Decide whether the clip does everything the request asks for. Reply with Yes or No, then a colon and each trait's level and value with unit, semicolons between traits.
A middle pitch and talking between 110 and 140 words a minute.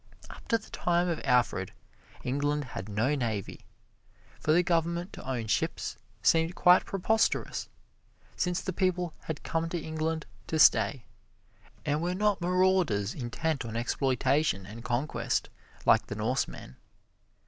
Yes: medium, 155 Hz; slow, 135 wpm